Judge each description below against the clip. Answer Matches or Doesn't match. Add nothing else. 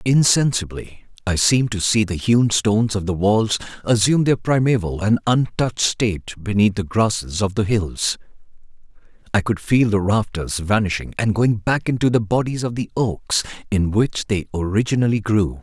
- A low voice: Matches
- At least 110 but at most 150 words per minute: Doesn't match